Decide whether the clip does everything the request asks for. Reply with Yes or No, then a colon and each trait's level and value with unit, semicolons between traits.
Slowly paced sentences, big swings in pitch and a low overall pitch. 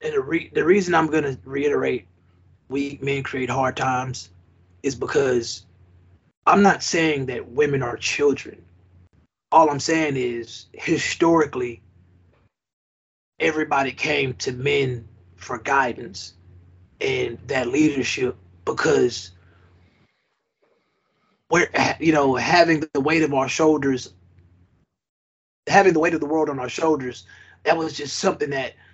Yes: slow, 125 wpm; wide, 8.7 semitones; low, 130 Hz